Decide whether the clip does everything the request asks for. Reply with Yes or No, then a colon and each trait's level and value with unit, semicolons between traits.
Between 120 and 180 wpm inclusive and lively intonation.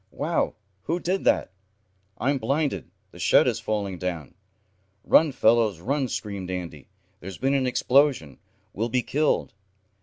Yes: average, 140 wpm; wide, 7.0 semitones